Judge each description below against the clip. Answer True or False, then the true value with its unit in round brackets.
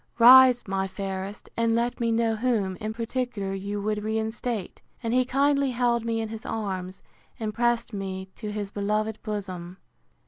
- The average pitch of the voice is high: True (220 Hz)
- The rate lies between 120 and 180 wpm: True (165 wpm)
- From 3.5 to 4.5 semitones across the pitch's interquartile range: False (3.0 semitones)